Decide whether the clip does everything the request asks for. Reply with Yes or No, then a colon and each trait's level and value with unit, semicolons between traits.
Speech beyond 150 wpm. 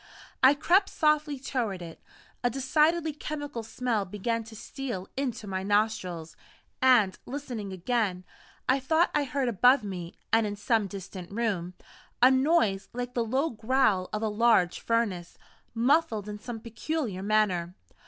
No: average, 145 wpm